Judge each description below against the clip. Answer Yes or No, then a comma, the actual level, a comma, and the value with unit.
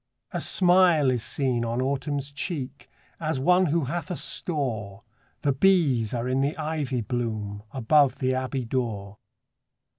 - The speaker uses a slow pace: No, average, 145 wpm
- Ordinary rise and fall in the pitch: Yes, average, 4.3 semitones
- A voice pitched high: No, low, 135 Hz